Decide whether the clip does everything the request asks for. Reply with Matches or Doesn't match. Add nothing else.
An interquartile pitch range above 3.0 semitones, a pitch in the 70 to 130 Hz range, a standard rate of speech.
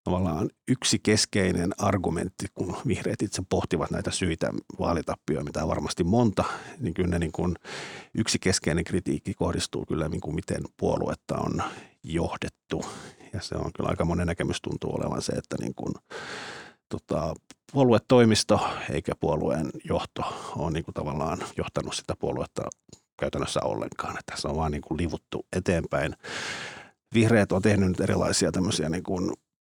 Matches